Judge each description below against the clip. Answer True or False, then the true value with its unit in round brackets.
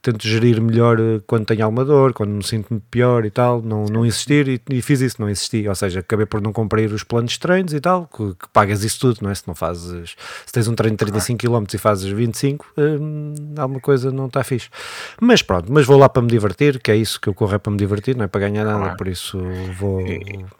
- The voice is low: True (110 Hz)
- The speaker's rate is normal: False (245 wpm)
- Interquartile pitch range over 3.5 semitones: True (3.9 semitones)